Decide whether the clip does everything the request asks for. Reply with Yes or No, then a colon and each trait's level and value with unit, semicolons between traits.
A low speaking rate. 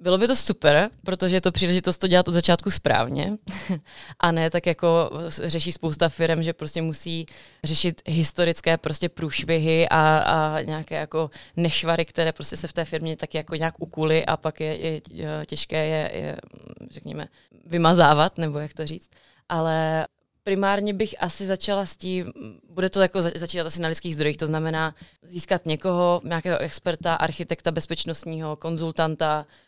No: average, 160 wpm